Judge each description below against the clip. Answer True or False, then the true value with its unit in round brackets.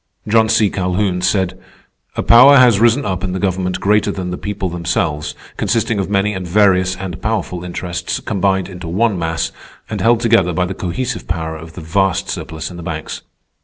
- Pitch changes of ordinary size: True (3.0 semitones)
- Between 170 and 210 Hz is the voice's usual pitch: False (95 Hz)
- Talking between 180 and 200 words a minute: True (190 wpm)